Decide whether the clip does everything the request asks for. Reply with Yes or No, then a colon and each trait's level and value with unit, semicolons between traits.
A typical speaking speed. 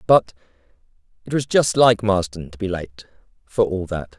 Yes: average, 170 wpm